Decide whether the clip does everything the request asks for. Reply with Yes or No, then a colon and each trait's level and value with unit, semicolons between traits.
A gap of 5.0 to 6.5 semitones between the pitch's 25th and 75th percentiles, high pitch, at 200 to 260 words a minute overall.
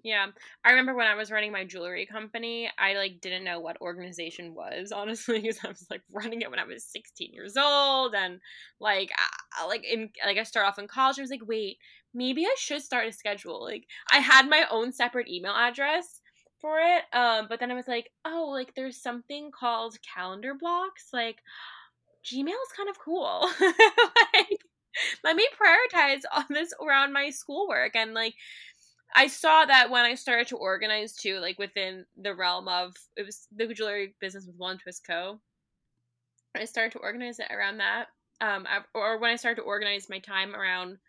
No: wide, 5.6 semitones; high, 230 Hz; average, 190 wpm